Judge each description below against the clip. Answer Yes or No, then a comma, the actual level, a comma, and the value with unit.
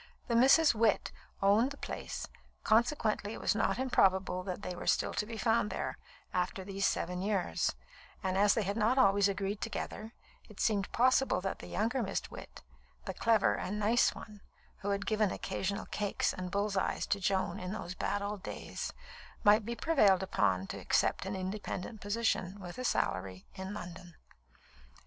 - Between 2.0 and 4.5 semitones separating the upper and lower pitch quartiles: Yes, average, 2.7 semitones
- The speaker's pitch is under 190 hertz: No, high, 205 Hz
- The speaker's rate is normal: Yes, average, 175 wpm